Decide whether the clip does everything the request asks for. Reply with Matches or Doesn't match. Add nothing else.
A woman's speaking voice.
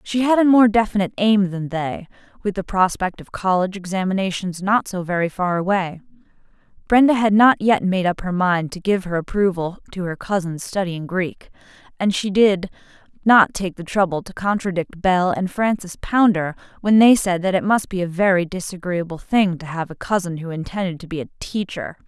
Matches